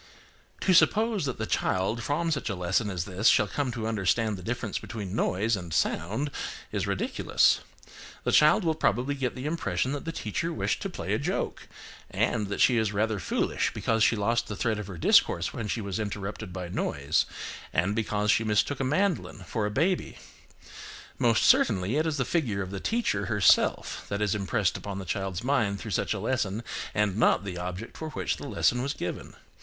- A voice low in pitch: Yes, low, 110 Hz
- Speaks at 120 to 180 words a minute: No, average, 200 wpm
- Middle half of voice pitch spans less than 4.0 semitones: No, average, 4.8 semitones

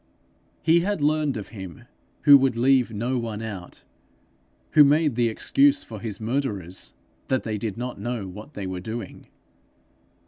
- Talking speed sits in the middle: Yes, average, 160 wpm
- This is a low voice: Yes, low, 115 Hz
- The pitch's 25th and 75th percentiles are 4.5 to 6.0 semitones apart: Yes, average, 5.1 semitones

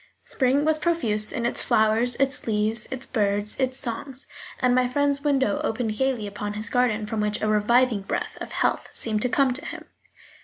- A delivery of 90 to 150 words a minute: No, average, 190 wpm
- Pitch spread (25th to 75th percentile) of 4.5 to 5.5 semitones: No, average, 3.8 semitones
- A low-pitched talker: No, high, 240 Hz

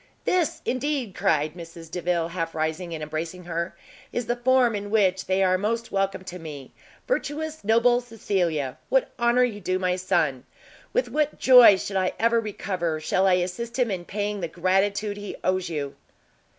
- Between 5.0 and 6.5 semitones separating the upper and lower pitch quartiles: Yes, average, 5.3 semitones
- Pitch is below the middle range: No, high, 190 Hz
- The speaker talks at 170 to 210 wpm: Yes, average, 175 wpm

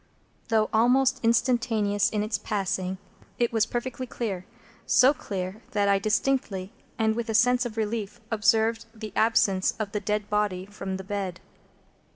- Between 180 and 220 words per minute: No, average, 155 wpm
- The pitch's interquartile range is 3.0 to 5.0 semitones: No, narrow, 2.5 semitones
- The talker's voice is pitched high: Yes, high, 215 Hz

